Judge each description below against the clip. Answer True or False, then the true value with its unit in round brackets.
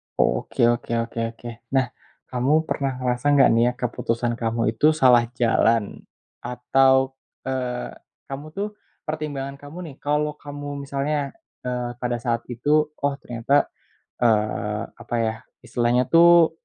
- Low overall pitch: True (130 Hz)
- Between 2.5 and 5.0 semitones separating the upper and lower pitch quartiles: True (3.3 semitones)